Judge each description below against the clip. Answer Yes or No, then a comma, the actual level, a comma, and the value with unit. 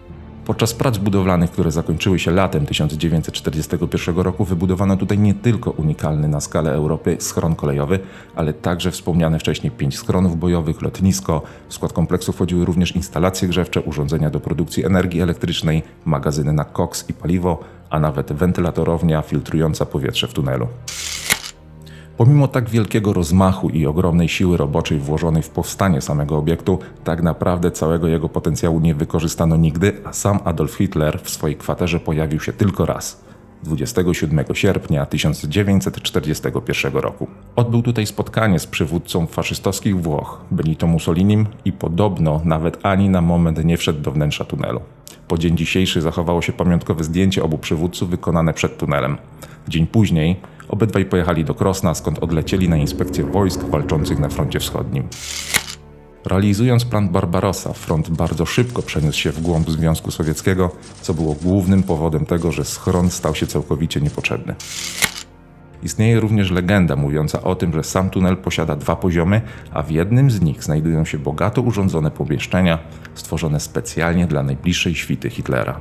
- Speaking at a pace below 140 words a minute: No, average, 145 wpm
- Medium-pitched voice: No, very low, 85 Hz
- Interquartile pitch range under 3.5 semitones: Yes, average, 3.1 semitones